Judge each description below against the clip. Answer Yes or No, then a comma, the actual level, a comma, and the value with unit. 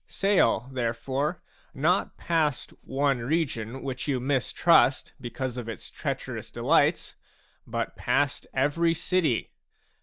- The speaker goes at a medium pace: No, slow, 110 wpm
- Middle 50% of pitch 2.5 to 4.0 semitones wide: No, average, 4.5 semitones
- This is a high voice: No, low, 135 Hz